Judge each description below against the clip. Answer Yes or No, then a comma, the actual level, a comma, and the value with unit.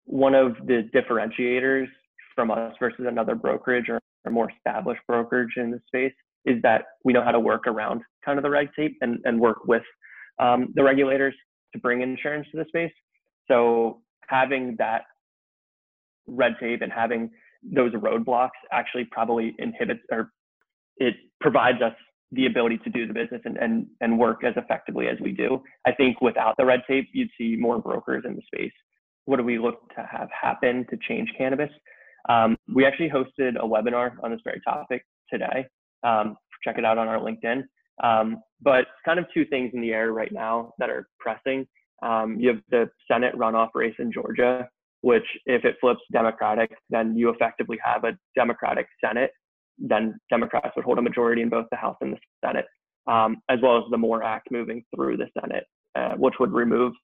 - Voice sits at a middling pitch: No, low, 120 Hz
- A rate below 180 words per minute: No, average, 185 wpm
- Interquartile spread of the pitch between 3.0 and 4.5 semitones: No, narrow, 2.6 semitones